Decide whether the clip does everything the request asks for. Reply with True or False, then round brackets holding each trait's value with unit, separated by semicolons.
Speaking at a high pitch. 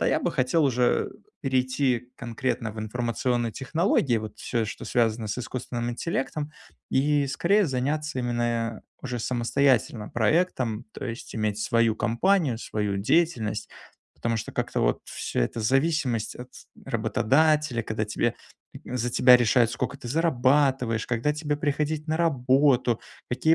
False (125 Hz)